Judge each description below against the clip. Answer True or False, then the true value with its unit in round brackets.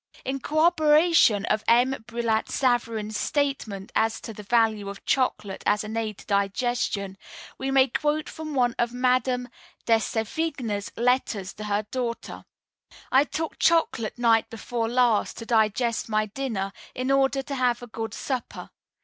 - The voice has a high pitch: True (235 Hz)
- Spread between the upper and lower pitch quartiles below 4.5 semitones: True (3.6 semitones)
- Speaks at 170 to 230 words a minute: False (150 wpm)